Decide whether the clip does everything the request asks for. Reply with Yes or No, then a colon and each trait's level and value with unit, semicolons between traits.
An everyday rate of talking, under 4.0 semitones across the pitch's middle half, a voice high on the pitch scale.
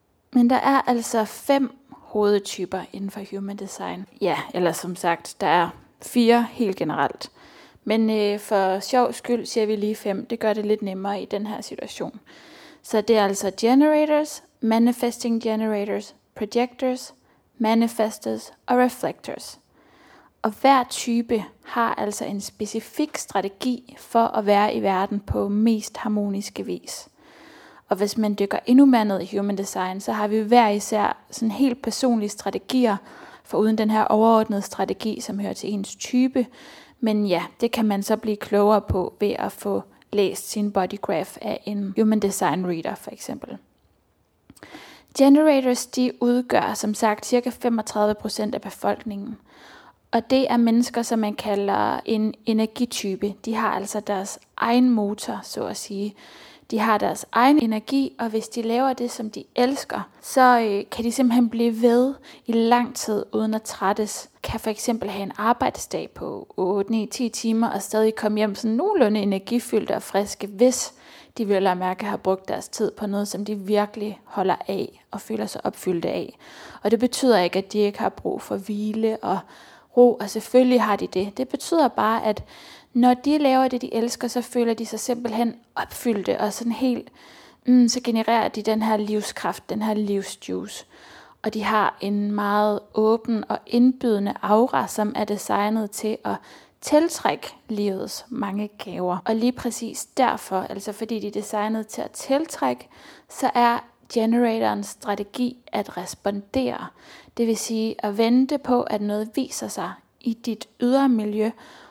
Yes: average, 165 wpm; average, 2.9 semitones; high, 220 Hz